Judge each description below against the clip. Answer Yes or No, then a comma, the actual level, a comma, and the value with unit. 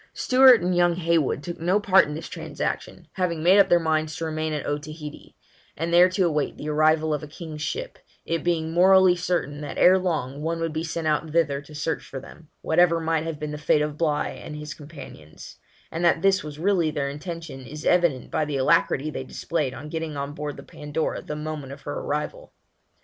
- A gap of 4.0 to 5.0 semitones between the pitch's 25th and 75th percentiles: No, narrow, 2.4 semitones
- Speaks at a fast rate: Yes, fast, 215 wpm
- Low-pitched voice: No, medium, 155 Hz